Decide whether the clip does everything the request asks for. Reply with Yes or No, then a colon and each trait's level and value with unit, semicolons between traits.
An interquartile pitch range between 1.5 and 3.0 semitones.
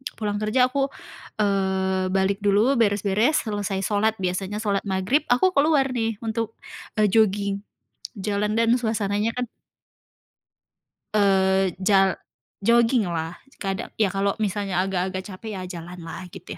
Yes: average, 2.7 semitones